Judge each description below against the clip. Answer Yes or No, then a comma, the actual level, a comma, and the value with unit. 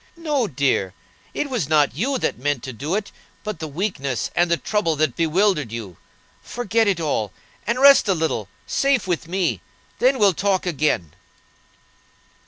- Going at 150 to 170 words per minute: Yes, average, 165 wpm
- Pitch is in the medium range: Yes, medium, 170 Hz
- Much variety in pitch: Yes, wide, 7.0 semitones